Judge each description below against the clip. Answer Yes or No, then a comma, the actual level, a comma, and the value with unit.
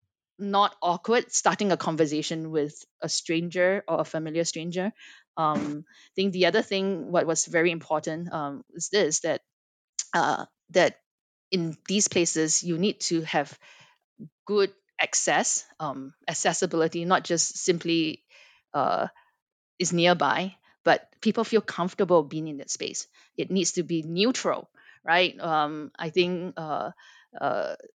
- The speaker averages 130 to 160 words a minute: Yes, slow, 135 wpm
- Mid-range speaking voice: Yes, medium, 170 Hz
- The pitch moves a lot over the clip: No, average, 3.3 semitones